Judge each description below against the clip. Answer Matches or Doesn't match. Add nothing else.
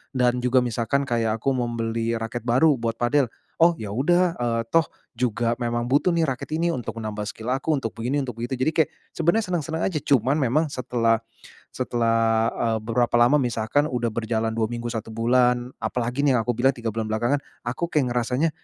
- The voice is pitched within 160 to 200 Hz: Doesn't match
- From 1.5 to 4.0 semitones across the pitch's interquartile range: Matches